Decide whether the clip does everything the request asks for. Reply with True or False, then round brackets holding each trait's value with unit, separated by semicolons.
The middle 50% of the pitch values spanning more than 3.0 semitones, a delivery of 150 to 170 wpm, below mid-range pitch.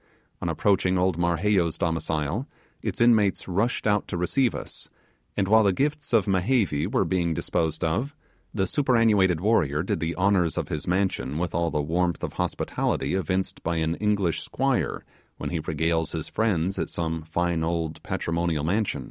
True (4.0 semitones; 165 wpm; 90 Hz)